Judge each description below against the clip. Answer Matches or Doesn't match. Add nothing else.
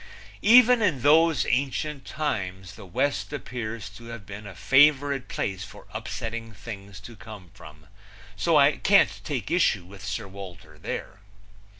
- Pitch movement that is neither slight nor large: Doesn't match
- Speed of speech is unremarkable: Matches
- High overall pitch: Doesn't match